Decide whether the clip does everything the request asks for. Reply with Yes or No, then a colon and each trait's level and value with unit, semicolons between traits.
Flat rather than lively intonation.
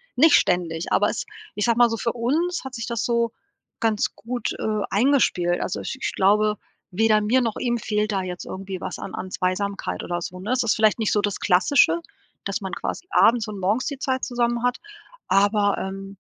No: average, 3.6 semitones